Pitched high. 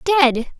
Yes: very high, 300 Hz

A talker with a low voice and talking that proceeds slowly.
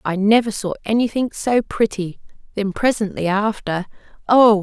No: high, 210 Hz; slow, 130 wpm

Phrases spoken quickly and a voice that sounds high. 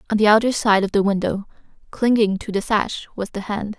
Yes: fast, 220 wpm; high, 210 Hz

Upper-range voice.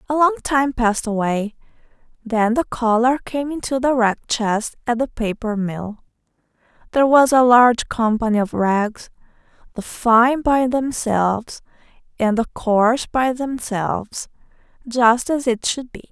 Yes: high, 235 Hz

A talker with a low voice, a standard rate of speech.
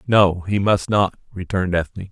Yes: very low, 95 Hz; average, 170 wpm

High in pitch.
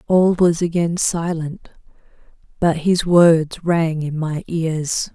No: medium, 165 Hz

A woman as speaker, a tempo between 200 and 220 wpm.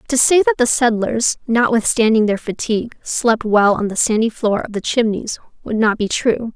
No: female; average, 190 wpm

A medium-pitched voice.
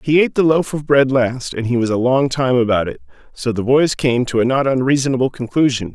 No: low, 130 Hz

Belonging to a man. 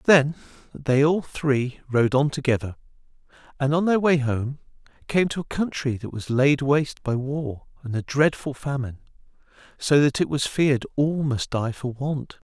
Yes: male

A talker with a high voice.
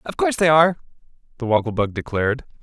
No: low, 135 Hz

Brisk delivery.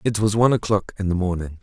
Yes: fast, 260 wpm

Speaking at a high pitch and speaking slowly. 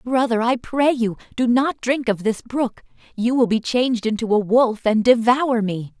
No: high, 235 Hz; average, 200 wpm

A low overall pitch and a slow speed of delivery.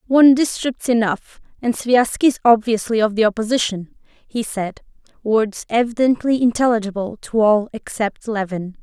No: high, 225 Hz; slow, 120 wpm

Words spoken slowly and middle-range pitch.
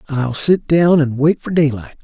No: fast, 205 wpm; medium, 145 Hz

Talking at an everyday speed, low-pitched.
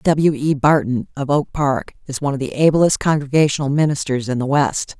No: average, 190 wpm; medium, 145 Hz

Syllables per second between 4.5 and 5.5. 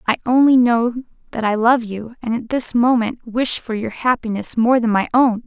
Yes: 4.9 syllables/s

